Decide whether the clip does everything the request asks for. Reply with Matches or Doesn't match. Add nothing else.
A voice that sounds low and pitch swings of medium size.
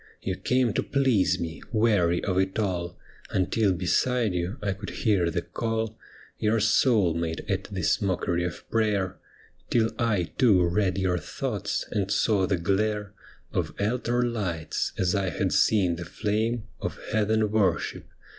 Matches